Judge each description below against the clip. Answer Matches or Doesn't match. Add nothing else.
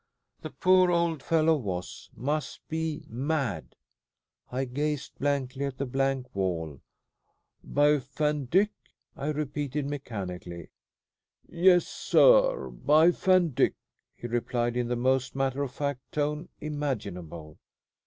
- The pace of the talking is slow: Matches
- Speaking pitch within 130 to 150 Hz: Matches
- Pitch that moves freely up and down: Doesn't match